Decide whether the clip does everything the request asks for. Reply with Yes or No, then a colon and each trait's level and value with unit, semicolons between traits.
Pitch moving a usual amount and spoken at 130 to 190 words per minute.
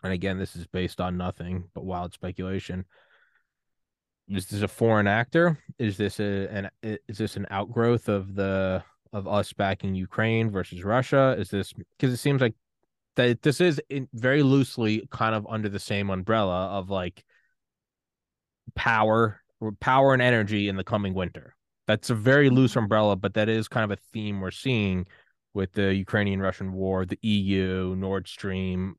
Yes: average, 3.1 semitones; average, 170 wpm